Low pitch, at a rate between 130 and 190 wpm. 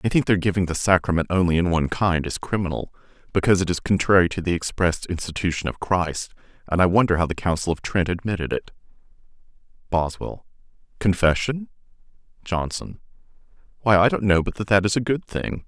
Yes: very low, 90 Hz; average, 170 wpm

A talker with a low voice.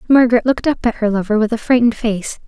No: high, 230 Hz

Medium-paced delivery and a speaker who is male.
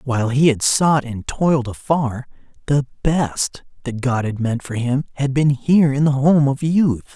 Yes: average, 195 wpm; male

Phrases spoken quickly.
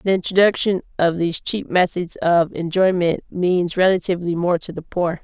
No: average, 160 wpm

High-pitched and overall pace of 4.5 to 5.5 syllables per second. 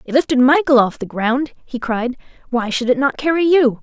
Yes: very high, 260 Hz; 5.1 syllables/s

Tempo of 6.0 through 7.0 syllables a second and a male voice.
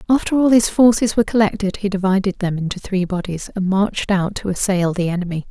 No: 6.1 syllables/s; female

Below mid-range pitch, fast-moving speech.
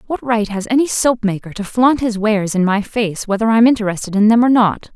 No: high, 220 Hz; fast, 240 wpm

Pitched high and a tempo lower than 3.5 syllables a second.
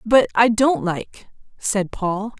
Yes: high, 215 Hz; 3.2 syllables/s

